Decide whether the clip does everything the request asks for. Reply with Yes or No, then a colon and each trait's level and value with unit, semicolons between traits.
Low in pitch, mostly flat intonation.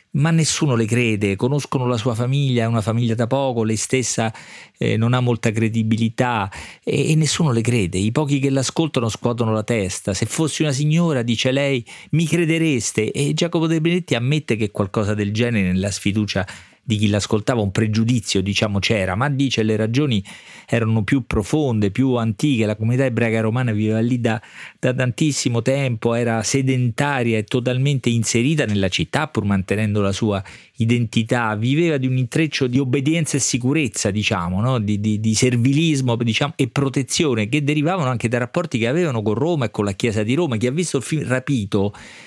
No: low, 120 Hz; average, 4.2 semitones